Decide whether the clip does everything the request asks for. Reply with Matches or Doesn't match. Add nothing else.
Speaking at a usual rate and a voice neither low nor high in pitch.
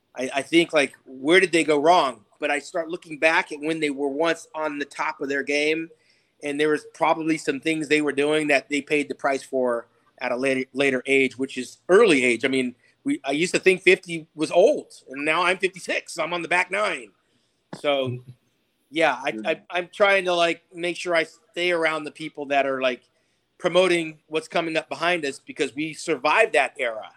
Doesn't match